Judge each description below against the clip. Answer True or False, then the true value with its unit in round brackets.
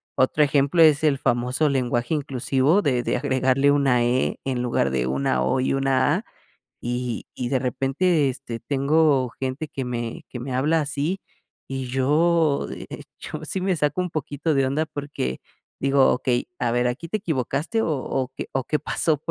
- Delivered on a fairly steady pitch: False (3.3 semitones)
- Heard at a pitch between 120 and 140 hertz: True (135 Hz)